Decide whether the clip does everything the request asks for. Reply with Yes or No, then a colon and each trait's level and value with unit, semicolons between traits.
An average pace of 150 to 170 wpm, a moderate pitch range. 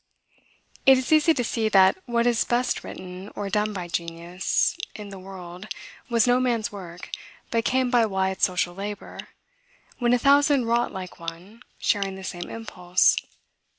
Yes: average, 160 wpm; average, 4.5 semitones